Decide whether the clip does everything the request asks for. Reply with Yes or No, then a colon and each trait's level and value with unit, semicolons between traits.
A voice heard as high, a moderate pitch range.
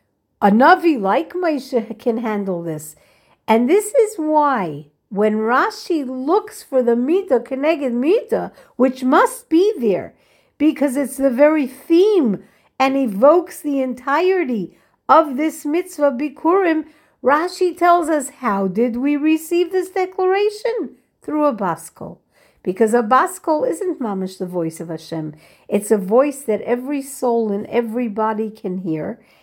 No: very high, 275 Hz; wide, 7.0 semitones